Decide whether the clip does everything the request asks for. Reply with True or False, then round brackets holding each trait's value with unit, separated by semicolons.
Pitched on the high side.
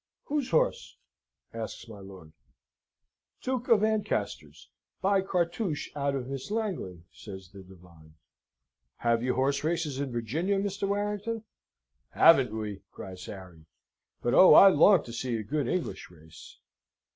False (135 Hz)